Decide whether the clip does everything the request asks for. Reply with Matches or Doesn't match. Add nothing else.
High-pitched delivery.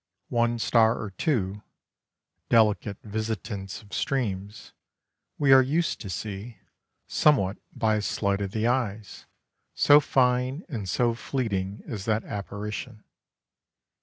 Doesn't match